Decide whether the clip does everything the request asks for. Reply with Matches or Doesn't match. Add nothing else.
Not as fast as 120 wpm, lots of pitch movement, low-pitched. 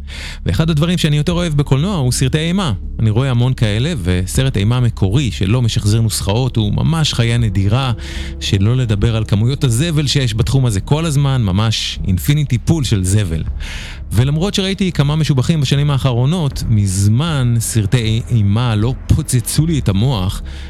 Doesn't match